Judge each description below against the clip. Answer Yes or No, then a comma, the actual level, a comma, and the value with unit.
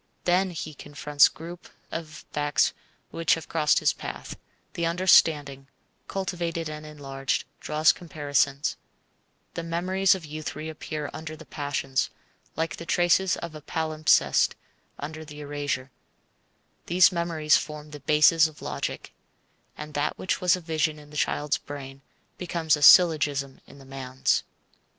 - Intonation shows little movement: Yes, narrow, 2.3 semitones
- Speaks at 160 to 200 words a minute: No, average, 140 wpm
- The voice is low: No, medium, 155 Hz